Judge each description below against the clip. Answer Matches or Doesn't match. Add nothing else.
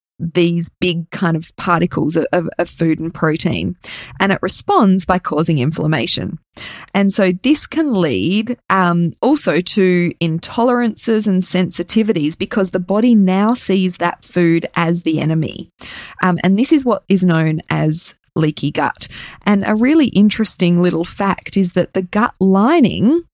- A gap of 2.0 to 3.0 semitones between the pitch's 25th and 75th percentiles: Doesn't match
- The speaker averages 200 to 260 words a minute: Doesn't match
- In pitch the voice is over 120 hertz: Matches